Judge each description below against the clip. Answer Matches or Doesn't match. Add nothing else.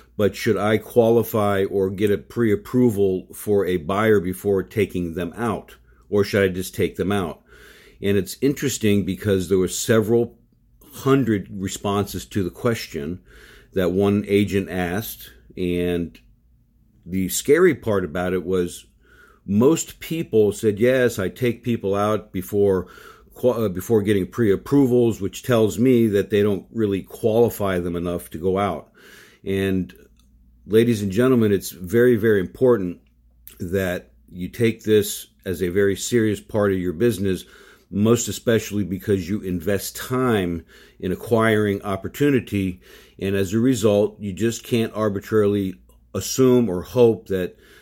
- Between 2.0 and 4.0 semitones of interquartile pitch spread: Matches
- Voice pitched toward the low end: Matches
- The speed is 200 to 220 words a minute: Doesn't match